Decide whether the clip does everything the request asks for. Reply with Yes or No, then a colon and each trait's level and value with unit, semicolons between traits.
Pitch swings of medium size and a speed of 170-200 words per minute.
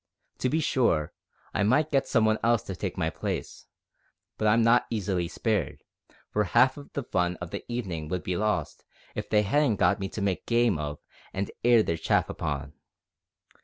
Yes: average, 5.0 semitones; average, 185 wpm